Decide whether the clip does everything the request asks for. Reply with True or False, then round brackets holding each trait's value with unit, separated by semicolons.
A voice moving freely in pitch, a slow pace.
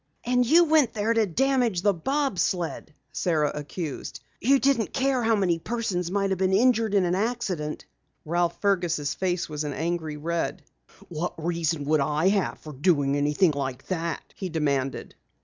False (6.2 semitones; 165 wpm)